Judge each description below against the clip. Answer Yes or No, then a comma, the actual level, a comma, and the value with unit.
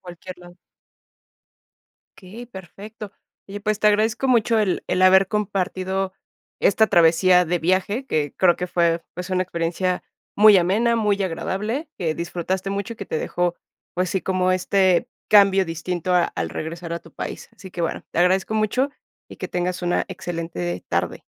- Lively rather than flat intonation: No, average, 2.7 semitones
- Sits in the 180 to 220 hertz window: Yes, medium, 185 Hz